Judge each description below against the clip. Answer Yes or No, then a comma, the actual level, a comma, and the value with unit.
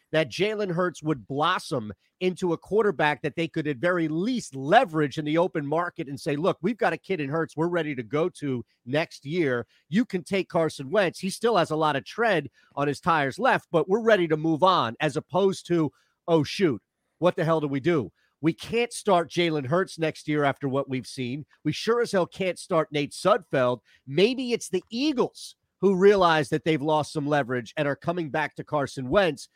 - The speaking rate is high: Yes, fast, 215 wpm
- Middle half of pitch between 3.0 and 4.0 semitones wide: Yes, average, 3.7 semitones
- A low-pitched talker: No, medium, 160 Hz